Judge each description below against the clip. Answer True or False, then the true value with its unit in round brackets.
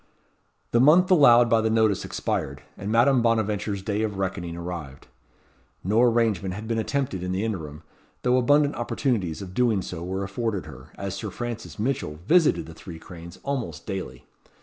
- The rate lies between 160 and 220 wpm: True (170 wpm)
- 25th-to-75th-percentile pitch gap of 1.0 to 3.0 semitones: False (4.7 semitones)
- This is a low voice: True (105 Hz)